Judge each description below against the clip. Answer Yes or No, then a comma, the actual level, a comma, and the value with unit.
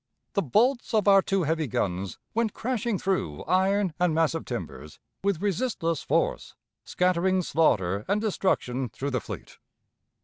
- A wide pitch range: Yes, wide, 6.3 semitones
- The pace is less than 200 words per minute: Yes, average, 140 wpm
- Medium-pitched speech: Yes, medium, 180 Hz